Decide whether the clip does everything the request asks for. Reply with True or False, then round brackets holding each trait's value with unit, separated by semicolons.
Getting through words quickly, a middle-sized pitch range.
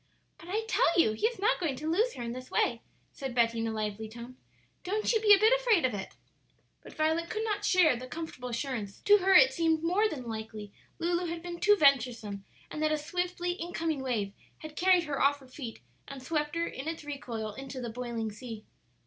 False (220 wpm; 6.7 semitones)